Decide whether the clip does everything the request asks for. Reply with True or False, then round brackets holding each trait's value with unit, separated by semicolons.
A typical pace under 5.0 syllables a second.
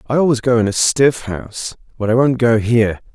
False (5.6 syllables/s)